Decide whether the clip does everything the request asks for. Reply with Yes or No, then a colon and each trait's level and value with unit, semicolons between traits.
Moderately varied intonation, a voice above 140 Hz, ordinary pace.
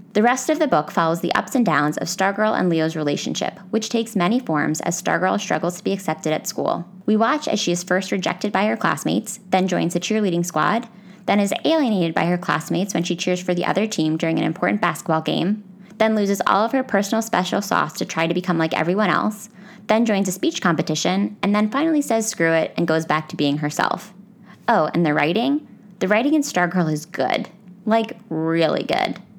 No: average, 4.5 semitones; medium, 185 Hz; fast, 215 wpm